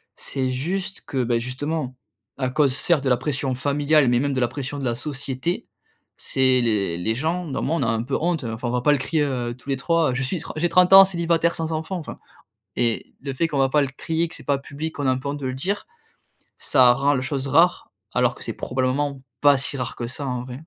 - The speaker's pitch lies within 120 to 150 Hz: Yes, medium, 140 Hz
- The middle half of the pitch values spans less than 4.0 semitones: Yes, average, 3.6 semitones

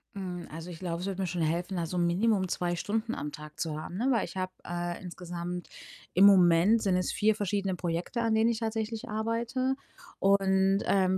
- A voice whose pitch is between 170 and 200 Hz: Yes, high, 190 Hz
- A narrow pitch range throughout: No, average, 3.8 semitones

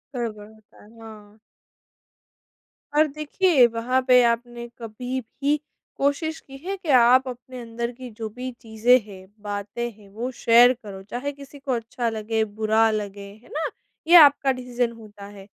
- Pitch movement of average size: Yes, average, 3.2 semitones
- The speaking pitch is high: Yes, high, 235 Hz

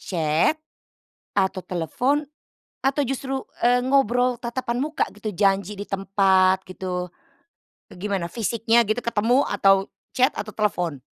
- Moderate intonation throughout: Yes, average, 4.6 semitones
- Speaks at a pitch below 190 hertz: No, high, 210 Hz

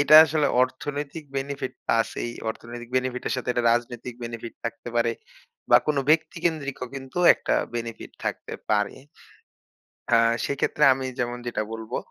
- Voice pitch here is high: No, low, 125 Hz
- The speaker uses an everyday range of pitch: Yes, average, 3.2 semitones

